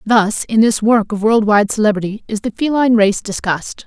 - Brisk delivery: No, average, 185 wpm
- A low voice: No, high, 215 Hz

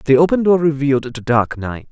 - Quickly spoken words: Yes, fast, 220 wpm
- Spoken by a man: Yes, male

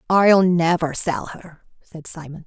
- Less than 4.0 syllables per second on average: Yes, 3.8 syllables/s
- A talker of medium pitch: Yes, medium, 170 Hz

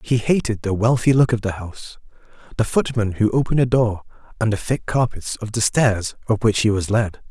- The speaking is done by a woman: No, male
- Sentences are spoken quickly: Yes, fast, 215 wpm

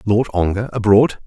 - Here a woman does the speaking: No, male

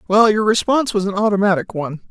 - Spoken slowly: No, average, 200 wpm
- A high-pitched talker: Yes, high, 205 Hz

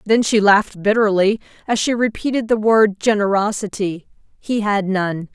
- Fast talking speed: No, slow, 135 wpm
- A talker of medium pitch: No, high, 210 Hz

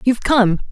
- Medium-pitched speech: No, high, 225 Hz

